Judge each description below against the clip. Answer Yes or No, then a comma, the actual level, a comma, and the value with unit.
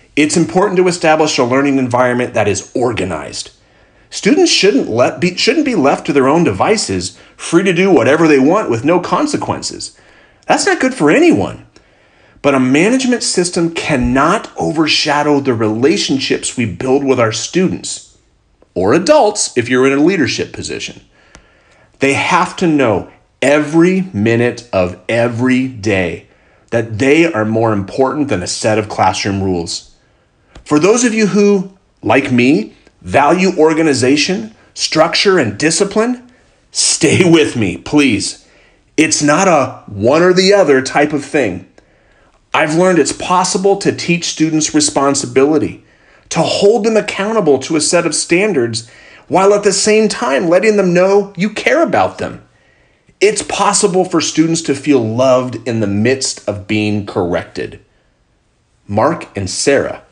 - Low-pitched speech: No, medium, 150 Hz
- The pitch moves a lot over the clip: Yes, wide, 7.3 semitones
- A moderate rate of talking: Yes, average, 145 wpm